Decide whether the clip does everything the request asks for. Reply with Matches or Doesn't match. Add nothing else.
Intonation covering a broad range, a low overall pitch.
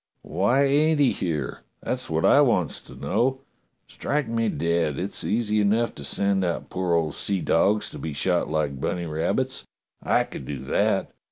Matches